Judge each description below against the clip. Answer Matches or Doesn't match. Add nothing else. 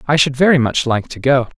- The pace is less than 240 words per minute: Doesn't match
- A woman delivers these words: Doesn't match